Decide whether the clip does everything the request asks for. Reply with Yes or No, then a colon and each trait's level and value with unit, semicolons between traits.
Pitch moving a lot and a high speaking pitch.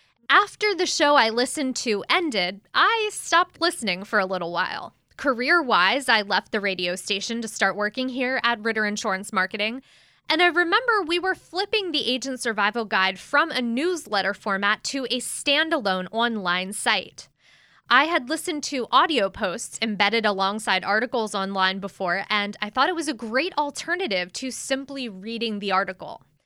Yes: wide, 6.9 semitones; high, 235 Hz